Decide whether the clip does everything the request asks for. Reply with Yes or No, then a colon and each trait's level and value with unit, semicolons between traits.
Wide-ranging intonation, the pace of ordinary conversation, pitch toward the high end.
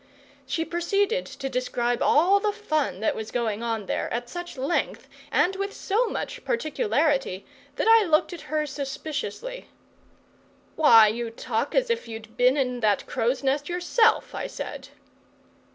Yes: wide, 8.6 semitones; average, 150 wpm; very high, 295 Hz